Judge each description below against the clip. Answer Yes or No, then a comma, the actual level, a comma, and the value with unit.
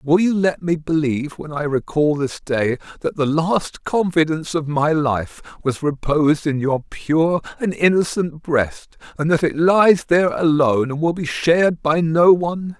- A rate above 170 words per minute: Yes, average, 180 wpm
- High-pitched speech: No, medium, 160 Hz